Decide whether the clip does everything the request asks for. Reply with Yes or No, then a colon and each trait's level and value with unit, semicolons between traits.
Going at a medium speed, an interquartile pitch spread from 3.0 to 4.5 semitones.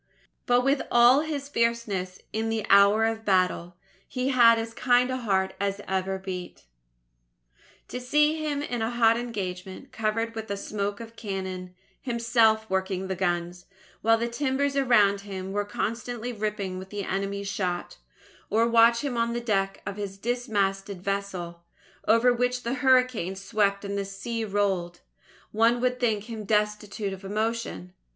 Yes: average, 160 wpm; average, 3.5 semitones